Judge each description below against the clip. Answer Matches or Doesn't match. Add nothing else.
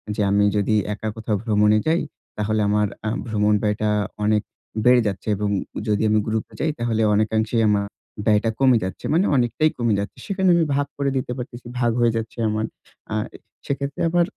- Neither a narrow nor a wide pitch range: Matches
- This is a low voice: Matches